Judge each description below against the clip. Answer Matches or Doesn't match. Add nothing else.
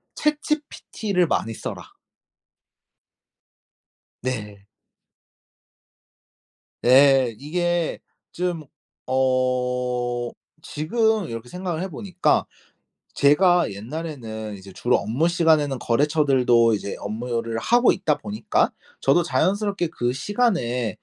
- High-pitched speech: Doesn't match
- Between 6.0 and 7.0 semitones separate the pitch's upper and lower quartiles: Matches